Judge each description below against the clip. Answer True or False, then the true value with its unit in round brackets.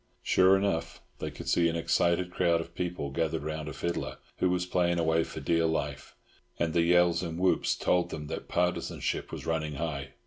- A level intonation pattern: True (1.8 semitones)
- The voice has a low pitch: True (85 Hz)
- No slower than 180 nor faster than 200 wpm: True (195 wpm)